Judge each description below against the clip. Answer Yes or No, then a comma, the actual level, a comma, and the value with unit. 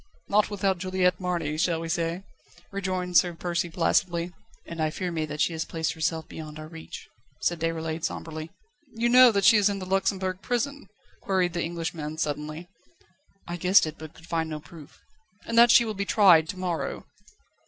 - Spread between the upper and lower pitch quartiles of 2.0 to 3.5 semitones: Yes, average, 2.8 semitones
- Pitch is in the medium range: Yes, medium, 175 Hz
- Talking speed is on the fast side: No, average, 185 wpm